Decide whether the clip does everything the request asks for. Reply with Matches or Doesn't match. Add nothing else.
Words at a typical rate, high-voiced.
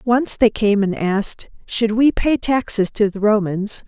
Matches